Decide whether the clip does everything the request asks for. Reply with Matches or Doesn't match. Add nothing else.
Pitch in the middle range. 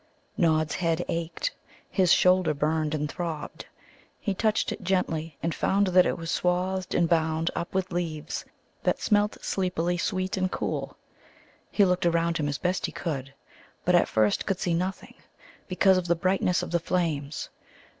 Matches